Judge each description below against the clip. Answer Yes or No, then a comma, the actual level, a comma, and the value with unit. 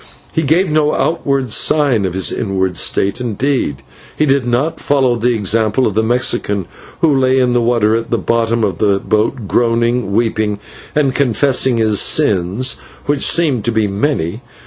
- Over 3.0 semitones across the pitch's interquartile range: Yes, average, 4.2 semitones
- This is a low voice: Yes, low, 120 Hz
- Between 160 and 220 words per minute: Yes, average, 170 wpm